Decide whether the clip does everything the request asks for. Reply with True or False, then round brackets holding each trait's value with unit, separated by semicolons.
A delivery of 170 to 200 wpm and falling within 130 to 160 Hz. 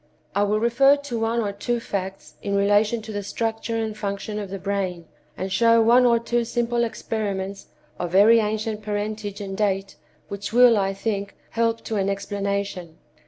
False (175 wpm; 210 Hz)